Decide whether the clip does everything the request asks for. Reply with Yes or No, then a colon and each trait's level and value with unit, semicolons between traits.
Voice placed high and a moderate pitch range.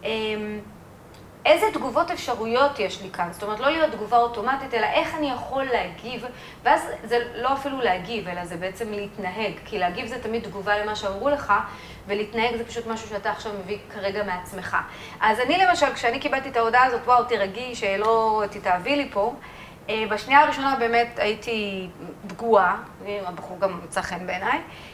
Yes: high, 220 Hz; average, 3.9 semitones